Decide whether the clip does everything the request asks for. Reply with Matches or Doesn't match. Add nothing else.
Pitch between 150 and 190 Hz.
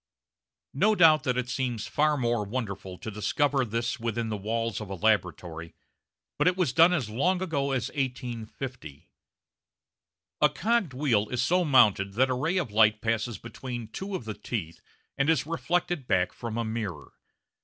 Doesn't match